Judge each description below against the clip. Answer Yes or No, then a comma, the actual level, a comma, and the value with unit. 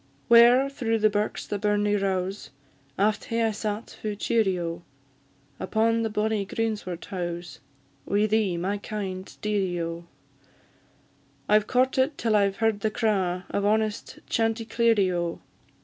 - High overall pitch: Yes, high, 210 Hz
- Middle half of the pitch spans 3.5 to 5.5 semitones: No, average, 2.7 semitones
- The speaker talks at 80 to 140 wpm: Yes, slow, 135 wpm